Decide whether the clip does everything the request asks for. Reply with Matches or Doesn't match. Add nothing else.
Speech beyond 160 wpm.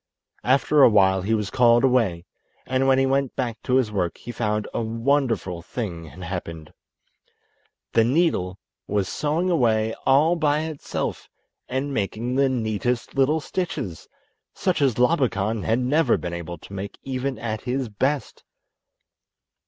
Doesn't match